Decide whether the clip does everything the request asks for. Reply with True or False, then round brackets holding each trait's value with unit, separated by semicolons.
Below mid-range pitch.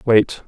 True (115 Hz)